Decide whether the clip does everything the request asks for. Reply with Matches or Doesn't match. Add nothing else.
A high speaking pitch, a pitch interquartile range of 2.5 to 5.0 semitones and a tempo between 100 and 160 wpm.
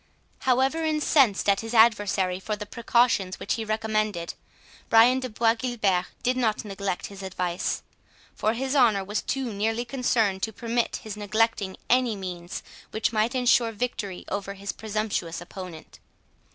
Matches